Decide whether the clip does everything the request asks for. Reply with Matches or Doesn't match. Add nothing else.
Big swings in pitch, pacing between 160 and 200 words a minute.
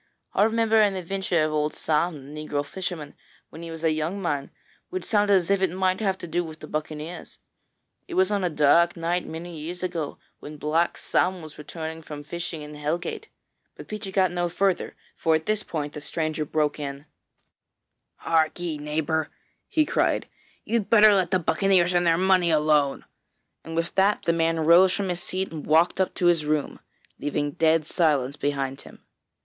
Doesn't match